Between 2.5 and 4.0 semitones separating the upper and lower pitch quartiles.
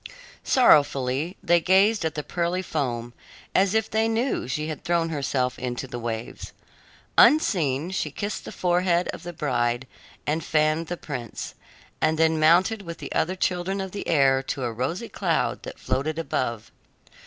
No: average, 5.3 semitones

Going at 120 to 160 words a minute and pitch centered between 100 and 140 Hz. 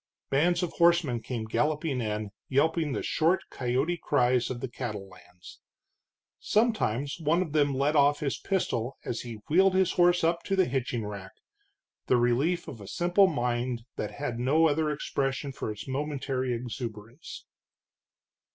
Yes: average, 155 wpm; low, 135 Hz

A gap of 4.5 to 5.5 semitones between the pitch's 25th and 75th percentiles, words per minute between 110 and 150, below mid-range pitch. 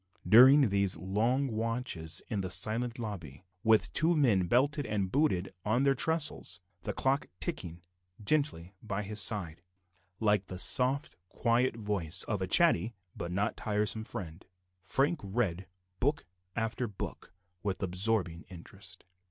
Yes: average, 5.2 semitones; average, 140 wpm; low, 105 Hz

